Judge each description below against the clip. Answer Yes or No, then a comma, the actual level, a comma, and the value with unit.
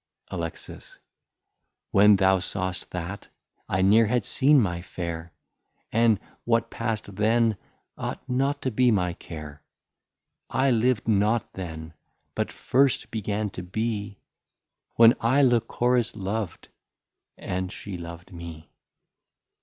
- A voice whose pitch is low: Yes, low, 105 Hz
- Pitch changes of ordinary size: Yes, average, 4.4 semitones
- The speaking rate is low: Yes, slow, 115 wpm